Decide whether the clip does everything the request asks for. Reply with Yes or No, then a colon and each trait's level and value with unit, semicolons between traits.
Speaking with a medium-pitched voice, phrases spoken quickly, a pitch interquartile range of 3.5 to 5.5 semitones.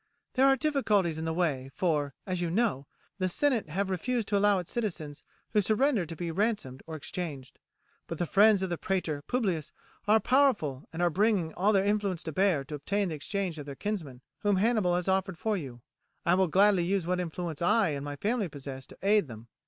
Yes: medium, 180 Hz; fast, 210 wpm; average, 4.7 semitones